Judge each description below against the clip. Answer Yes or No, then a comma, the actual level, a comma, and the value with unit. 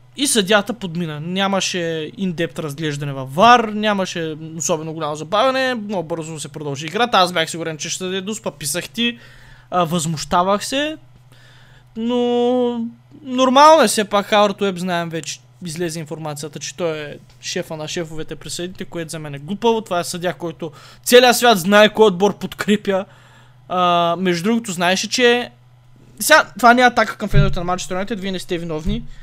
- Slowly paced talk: No, average, 160 wpm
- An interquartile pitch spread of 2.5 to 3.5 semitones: No, average, 5.0 semitones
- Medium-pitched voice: Yes, medium, 180 Hz